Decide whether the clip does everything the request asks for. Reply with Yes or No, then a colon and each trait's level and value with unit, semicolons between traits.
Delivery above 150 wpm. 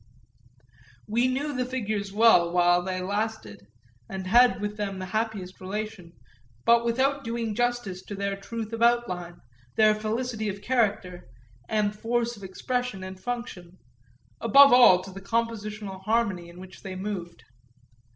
No: average, 145 wpm